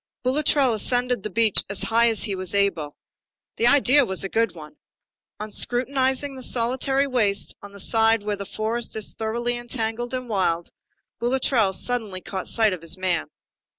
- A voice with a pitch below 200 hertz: No, high, 225 Hz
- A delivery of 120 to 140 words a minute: No, average, 170 wpm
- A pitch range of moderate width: Yes, average, 3.7 semitones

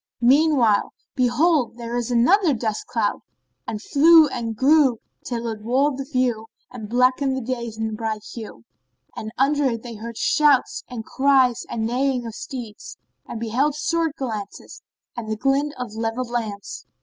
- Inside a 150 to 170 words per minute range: Yes, average, 155 wpm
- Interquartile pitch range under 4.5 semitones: Yes, average, 3.4 semitones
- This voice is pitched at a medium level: No, high, 245 Hz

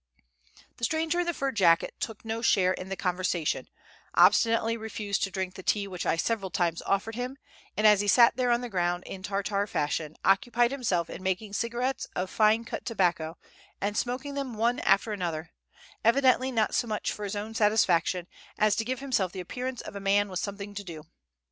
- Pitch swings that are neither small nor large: Yes, average, 4.0 semitones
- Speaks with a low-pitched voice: No, high, 205 Hz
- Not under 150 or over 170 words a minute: No, average, 200 wpm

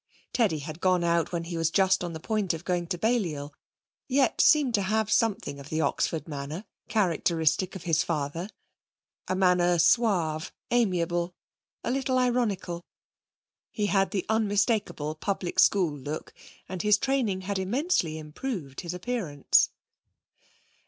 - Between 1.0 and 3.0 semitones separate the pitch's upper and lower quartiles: No, average, 4.6 semitones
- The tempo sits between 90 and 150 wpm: Yes, average, 145 wpm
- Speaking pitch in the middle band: Yes, medium, 180 Hz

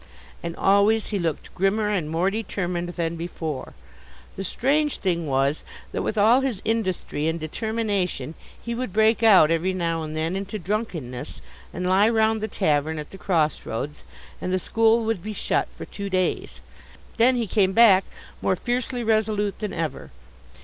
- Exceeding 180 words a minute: No, average, 165 wpm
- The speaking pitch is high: Yes, high, 195 Hz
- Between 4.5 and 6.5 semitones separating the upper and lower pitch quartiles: Yes, average, 4.8 semitones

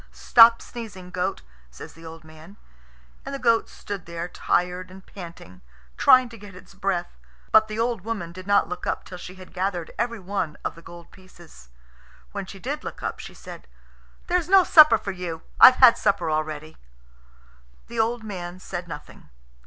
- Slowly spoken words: No, average, 175 wpm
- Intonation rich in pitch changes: No, average, 4.8 semitones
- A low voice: No, high, 190 Hz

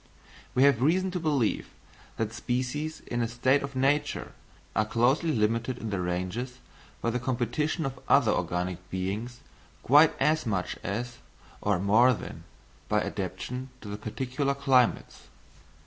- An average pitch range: Yes, average, 4.4 semitones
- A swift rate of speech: No, average, 140 wpm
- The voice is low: Yes, low, 125 Hz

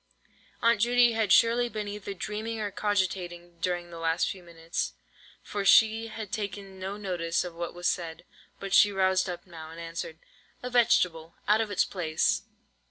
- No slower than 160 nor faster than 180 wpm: Yes, average, 170 wpm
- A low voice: No, high, 190 Hz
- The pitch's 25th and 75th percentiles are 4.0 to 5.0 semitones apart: No, average, 3.6 semitones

